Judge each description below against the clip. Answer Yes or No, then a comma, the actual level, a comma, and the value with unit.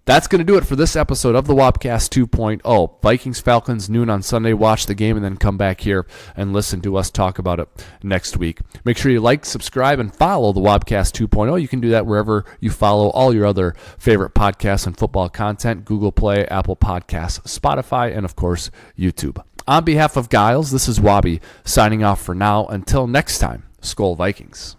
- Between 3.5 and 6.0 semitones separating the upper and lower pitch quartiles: Yes, average, 3.9 semitones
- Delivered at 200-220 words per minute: Yes, fast, 205 wpm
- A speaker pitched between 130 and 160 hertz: No, low, 105 Hz